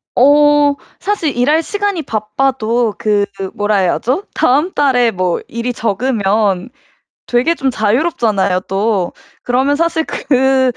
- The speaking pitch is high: Yes, high, 245 Hz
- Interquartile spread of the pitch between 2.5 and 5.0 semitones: No, wide, 5.4 semitones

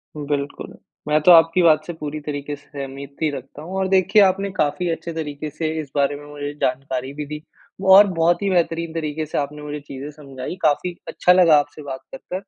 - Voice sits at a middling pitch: Yes, medium, 150 Hz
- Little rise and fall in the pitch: No, average, 3.0 semitones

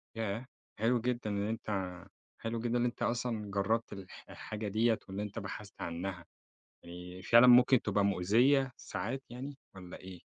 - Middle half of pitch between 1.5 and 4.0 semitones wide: Yes, average, 3.6 semitones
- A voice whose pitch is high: No, low, 105 Hz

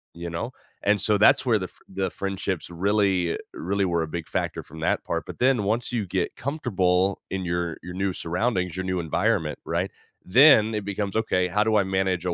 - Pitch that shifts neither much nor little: Yes, average, 3.0 semitones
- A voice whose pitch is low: Yes, very low, 95 Hz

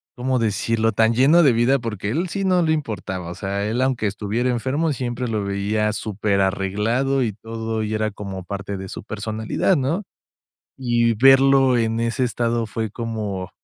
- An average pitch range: Yes, average, 3.7 semitones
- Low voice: Yes, low, 115 Hz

